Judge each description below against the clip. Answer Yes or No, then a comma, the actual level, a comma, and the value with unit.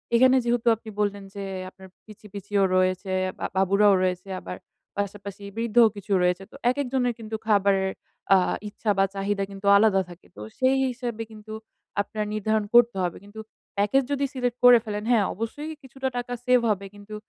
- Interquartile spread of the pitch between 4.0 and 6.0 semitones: No, average, 3.3 semitones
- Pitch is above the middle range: Yes, high, 210 Hz